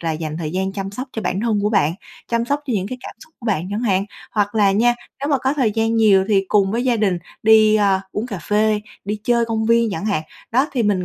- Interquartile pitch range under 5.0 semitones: Yes, average, 3.2 semitones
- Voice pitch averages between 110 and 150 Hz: No, high, 215 Hz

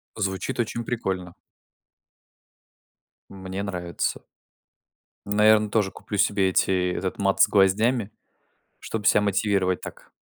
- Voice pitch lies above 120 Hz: No, low, 100 Hz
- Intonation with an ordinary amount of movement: No, narrow, 2.1 semitones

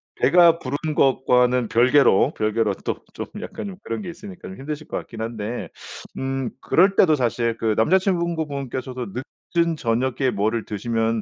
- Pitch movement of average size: No, wide, 5.9 semitones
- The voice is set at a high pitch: No, low, 130 Hz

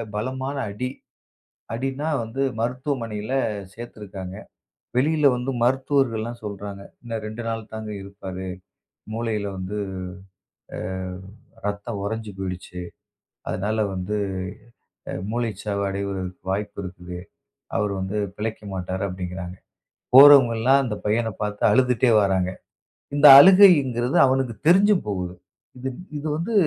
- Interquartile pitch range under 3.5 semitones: No, average, 4.7 semitones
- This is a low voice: Yes, low, 110 Hz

